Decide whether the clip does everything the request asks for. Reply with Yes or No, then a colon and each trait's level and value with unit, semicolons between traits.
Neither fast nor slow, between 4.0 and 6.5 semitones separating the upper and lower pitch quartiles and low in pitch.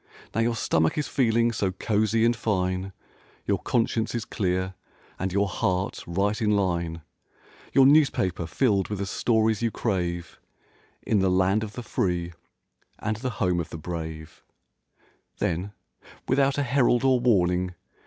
Yes: average, 150 wpm; average, 4.3 semitones; low, 100 Hz